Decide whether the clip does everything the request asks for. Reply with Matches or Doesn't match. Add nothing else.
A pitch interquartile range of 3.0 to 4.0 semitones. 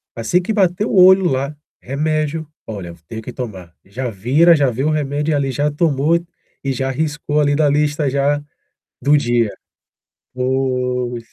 Matches